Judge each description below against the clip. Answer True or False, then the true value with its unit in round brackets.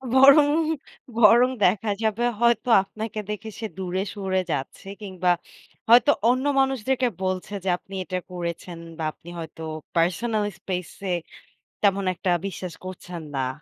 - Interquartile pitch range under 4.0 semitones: False (4.4 semitones)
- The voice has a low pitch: False (195 Hz)